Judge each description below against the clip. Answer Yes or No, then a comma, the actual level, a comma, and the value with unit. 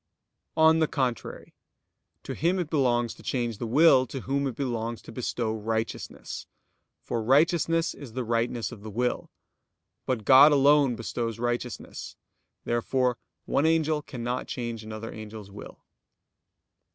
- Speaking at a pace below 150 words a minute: Yes, average, 140 wpm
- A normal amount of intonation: Yes, average, 3.6 semitones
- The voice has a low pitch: Yes, low, 125 Hz